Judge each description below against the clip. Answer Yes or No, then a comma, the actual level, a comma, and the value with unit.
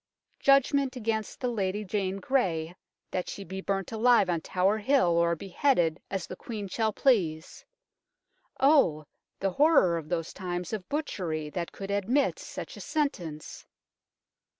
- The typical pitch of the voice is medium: No, high, 195 Hz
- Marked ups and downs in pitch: Yes, wide, 5.8 semitones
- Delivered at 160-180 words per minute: No, average, 150 wpm